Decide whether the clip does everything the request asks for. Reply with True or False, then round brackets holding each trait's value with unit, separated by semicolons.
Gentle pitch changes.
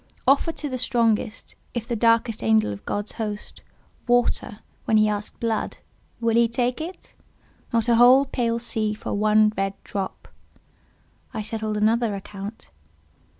True (2.1 semitones)